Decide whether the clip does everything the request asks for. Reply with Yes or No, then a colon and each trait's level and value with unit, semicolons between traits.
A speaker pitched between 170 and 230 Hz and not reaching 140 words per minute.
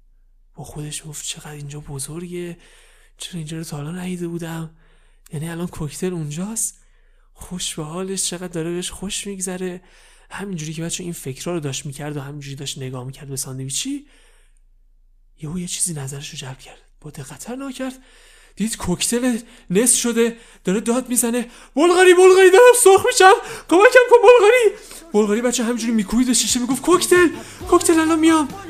No: medium, 185 Hz; fast, 155 wpm